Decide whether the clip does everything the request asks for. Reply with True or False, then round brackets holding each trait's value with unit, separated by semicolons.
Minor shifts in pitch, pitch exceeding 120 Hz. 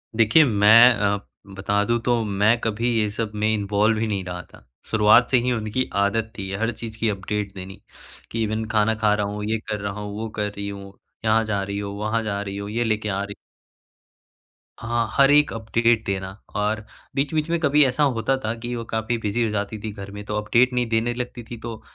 False (2.2 semitones; 110 Hz)